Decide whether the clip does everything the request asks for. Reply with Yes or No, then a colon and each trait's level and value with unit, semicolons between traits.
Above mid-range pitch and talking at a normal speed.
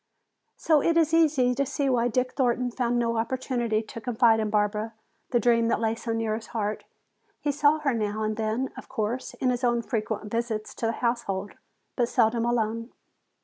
Yes: high, 235 Hz; average, 190 wpm